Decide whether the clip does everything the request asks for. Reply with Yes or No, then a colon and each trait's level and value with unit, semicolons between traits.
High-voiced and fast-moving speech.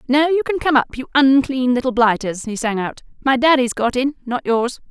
Yes: very high, 255 Hz; fast, 220 wpm